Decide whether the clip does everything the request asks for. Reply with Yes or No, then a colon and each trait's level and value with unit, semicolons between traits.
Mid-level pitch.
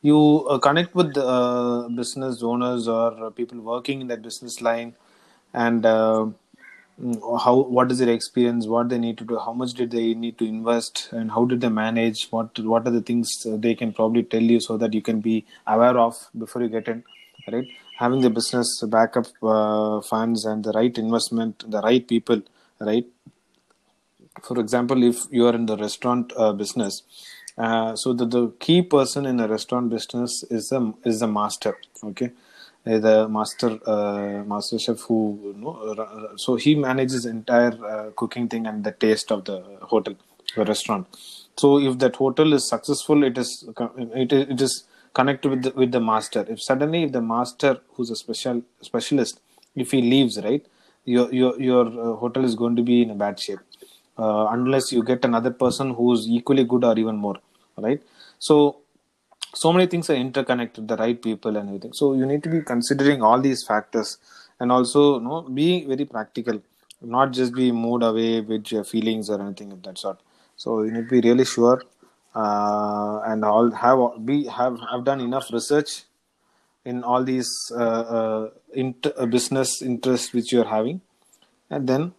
No: low, 120 Hz